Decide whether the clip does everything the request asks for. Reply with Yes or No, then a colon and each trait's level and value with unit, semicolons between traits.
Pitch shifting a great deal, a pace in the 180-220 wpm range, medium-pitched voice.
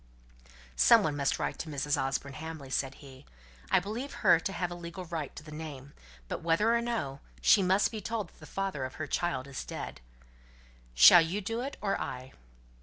Yes: wide, 5.8 semitones; average, 200 wpm; medium, 160 Hz